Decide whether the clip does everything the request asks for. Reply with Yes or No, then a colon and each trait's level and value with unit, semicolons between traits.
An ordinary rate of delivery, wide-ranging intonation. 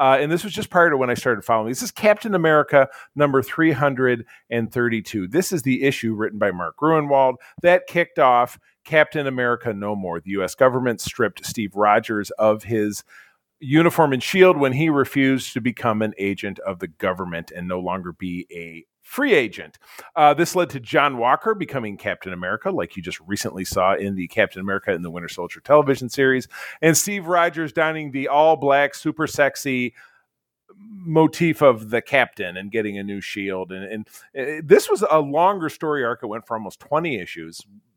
Yes: average, 185 wpm; wide, 6.8 semitones